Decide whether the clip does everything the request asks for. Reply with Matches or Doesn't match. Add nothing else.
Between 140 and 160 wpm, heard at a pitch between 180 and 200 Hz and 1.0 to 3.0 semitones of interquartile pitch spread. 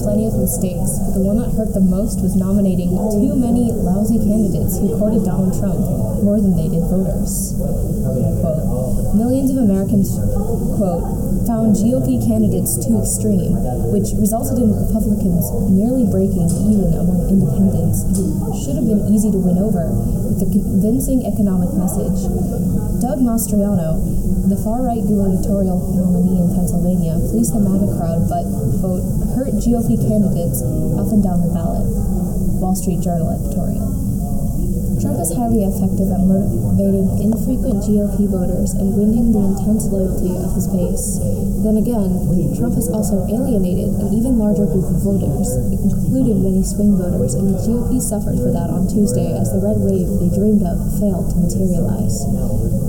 Matches